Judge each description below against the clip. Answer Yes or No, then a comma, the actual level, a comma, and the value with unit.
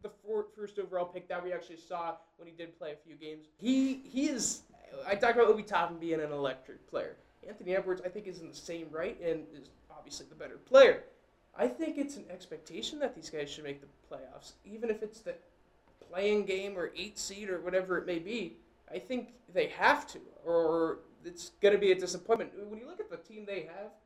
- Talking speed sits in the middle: No, fast, 220 wpm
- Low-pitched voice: No, medium, 185 Hz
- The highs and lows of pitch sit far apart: No, average, 4.4 semitones